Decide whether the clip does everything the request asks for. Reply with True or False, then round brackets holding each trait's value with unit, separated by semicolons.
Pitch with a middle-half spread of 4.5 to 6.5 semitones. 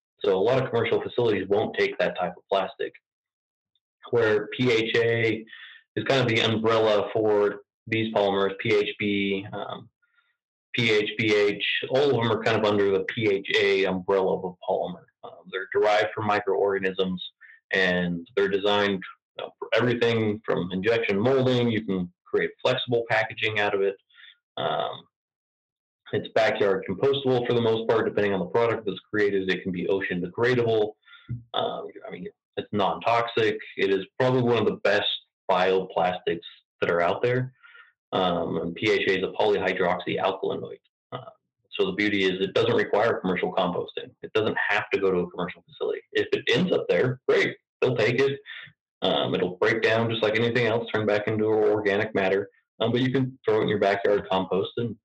True (5.3 semitones)